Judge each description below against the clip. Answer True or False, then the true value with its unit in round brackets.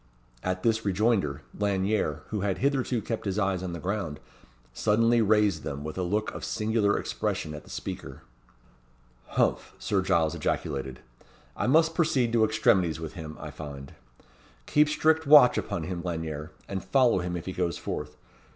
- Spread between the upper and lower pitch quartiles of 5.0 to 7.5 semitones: True (5.5 semitones)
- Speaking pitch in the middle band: False (95 Hz)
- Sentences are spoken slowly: False (165 wpm)